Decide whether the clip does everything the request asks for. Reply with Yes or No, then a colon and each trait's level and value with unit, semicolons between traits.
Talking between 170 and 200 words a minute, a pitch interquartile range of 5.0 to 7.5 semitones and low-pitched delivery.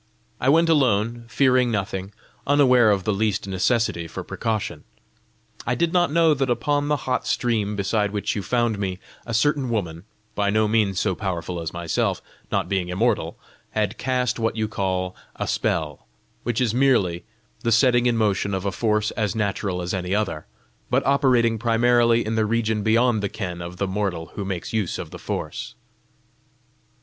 No: average, 175 wpm; average, 4.0 semitones; low, 110 Hz